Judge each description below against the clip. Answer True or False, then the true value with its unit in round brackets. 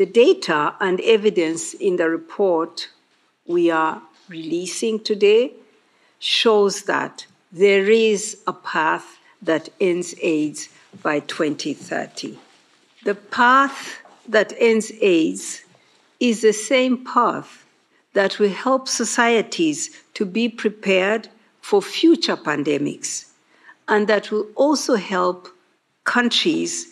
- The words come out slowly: True (105 wpm)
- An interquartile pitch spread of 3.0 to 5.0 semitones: False (5.5 semitones)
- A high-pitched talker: True (215 Hz)